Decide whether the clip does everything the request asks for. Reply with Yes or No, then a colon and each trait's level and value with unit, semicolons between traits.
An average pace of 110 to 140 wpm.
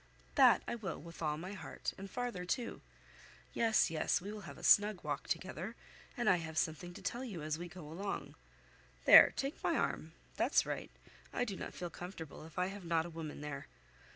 No: fast, 205 wpm